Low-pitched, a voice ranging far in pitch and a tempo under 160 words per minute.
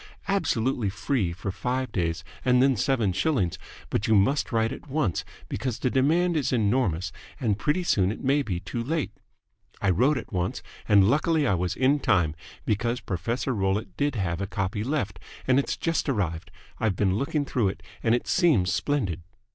No: low, 115 Hz; wide, 6.1 semitones; average, 180 wpm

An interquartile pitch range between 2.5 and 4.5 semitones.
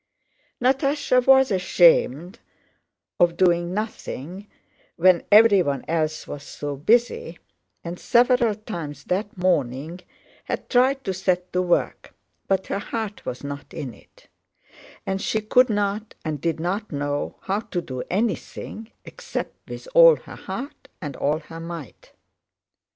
No: wide, 5.4 semitones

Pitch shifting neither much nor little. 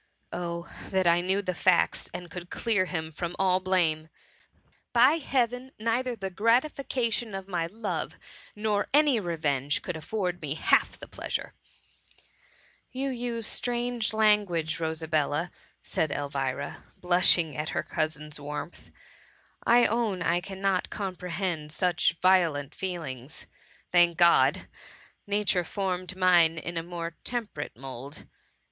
Yes: average, 4.7 semitones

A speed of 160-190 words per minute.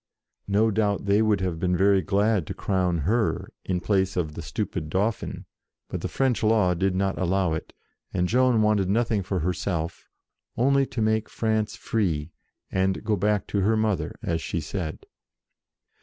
Yes: average, 170 wpm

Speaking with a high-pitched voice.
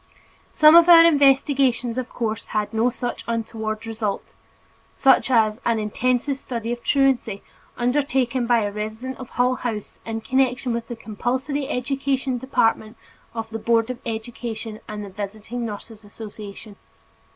Yes: high, 235 Hz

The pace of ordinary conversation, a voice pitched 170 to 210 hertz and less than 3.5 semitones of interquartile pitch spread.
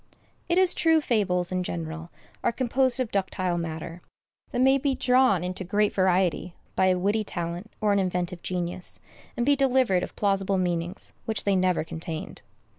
No: average, 170 wpm; high, 190 Hz; average, 4.9 semitones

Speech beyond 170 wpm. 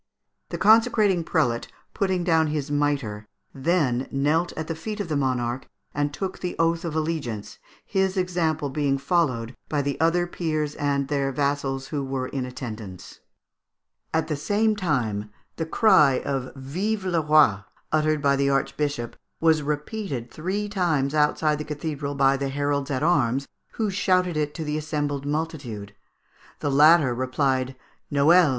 No: average, 155 wpm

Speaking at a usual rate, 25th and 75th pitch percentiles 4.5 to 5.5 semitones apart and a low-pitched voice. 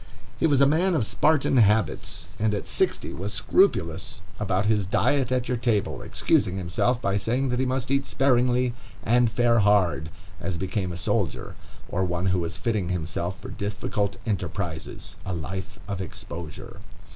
Yes: average, 165 wpm; average, 5.2 semitones; low, 105 Hz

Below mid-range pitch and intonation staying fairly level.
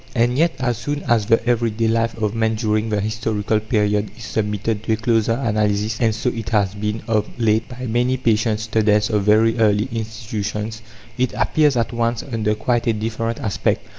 Yes: low, 110 Hz; narrow, 1.6 semitones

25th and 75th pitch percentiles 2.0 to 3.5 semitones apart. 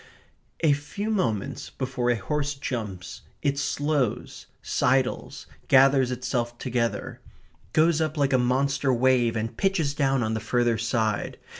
Yes: average, 3.2 semitones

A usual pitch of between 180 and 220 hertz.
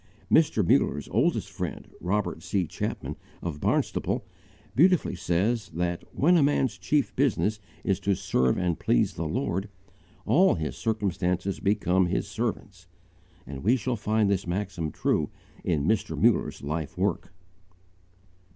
No: low, 100 Hz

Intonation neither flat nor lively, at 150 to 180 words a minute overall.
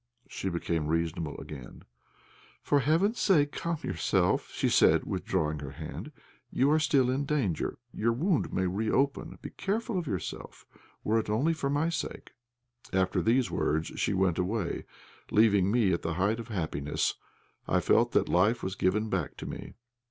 No: wide, 8.2 semitones; average, 165 wpm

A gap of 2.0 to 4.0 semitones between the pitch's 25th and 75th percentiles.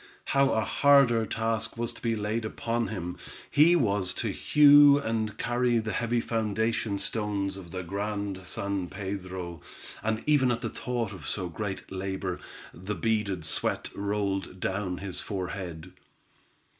Yes: average, 3.4 semitones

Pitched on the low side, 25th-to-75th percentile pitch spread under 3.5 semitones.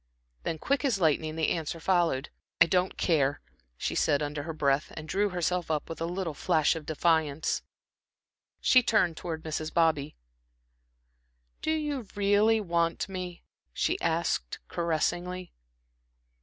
No: medium, 165 Hz; average, 3.0 semitones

